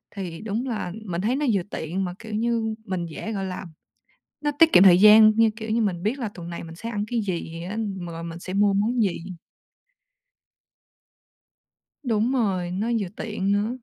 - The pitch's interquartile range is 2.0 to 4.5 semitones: Yes, average, 3.8 semitones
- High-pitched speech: Yes, high, 205 Hz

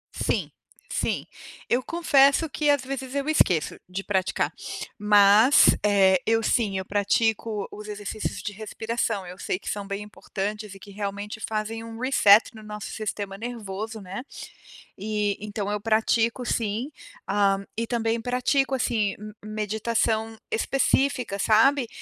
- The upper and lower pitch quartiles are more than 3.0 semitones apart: No, narrow, 2.4 semitones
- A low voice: No, high, 215 Hz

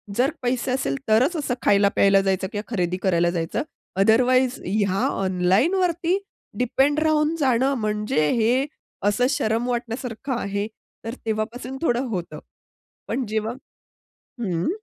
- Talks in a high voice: Yes, high, 230 Hz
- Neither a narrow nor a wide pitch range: Yes, average, 4.7 semitones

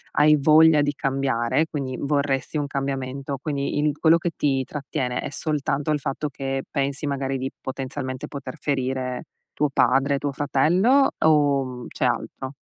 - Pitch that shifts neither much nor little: No, narrow, 1.9 semitones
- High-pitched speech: No, medium, 140 Hz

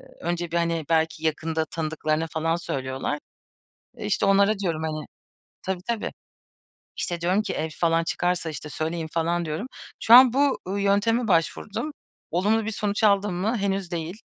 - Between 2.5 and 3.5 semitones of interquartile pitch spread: No, average, 3.9 semitones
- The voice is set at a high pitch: No, medium, 175 Hz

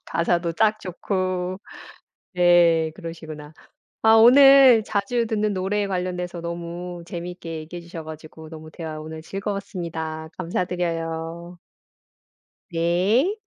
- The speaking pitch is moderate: Yes, medium, 175 Hz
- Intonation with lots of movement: No, average, 3.1 semitones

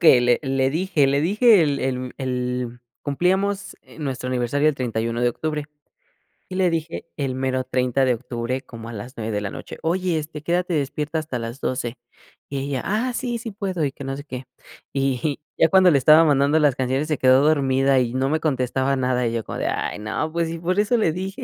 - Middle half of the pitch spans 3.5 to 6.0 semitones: Yes, average, 4.2 semitones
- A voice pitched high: No, medium, 140 Hz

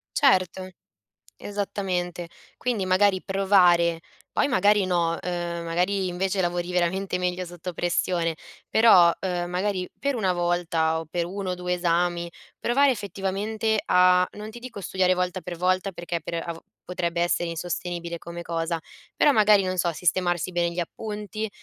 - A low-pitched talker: No, medium, 180 Hz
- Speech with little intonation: Yes, narrow, 2.2 semitones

